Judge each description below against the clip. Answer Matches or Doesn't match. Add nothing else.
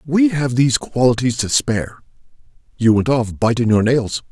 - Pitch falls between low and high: Doesn't match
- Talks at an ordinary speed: Matches